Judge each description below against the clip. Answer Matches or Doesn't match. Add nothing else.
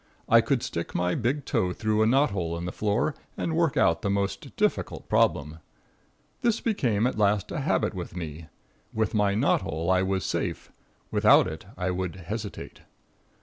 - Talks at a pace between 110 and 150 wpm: Doesn't match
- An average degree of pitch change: Matches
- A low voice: Matches